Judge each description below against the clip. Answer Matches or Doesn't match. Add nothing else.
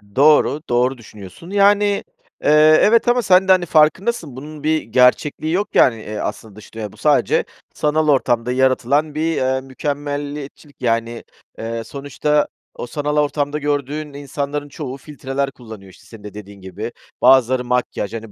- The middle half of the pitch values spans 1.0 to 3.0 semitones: Doesn't match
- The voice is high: Doesn't match